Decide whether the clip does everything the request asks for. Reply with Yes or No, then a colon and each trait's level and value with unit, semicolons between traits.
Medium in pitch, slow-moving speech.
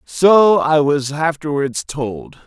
Yes: medium, 150 Hz; slow, 120 wpm